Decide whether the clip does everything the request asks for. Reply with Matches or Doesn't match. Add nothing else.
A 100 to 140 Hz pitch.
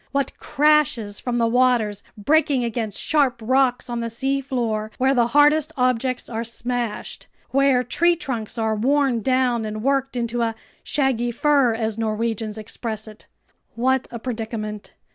Doesn't match